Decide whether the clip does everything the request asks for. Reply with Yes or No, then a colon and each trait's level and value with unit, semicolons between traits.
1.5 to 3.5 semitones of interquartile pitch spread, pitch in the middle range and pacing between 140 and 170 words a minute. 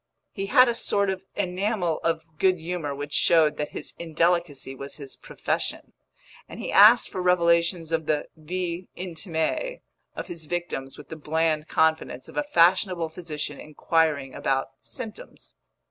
Yes: average, 3.0 semitones; medium, 165 Hz; average, 150 wpm